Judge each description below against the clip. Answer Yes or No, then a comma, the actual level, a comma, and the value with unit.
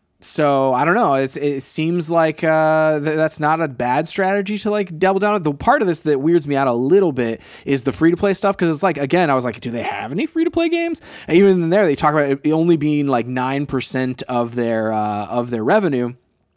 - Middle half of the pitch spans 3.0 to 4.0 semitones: No, average, 5.3 semitones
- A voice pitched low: No, medium, 150 Hz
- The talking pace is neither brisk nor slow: No, fast, 250 wpm